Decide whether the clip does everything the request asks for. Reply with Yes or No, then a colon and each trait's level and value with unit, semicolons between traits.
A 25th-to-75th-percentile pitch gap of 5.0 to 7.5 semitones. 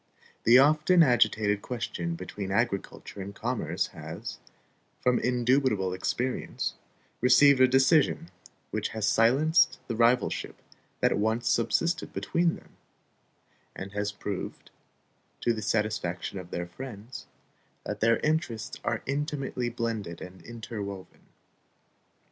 No: average, 4.3 semitones